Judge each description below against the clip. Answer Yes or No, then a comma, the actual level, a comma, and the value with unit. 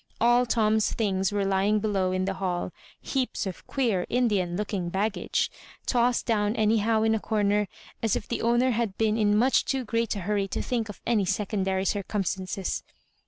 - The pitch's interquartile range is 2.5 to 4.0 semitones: Yes, average, 2.8 semitones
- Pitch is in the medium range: No, high, 210 Hz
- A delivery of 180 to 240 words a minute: Yes, average, 190 wpm